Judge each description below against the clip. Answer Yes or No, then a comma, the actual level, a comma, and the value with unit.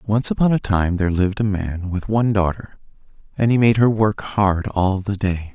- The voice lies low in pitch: Yes, low, 100 Hz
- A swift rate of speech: Yes, fast, 215 wpm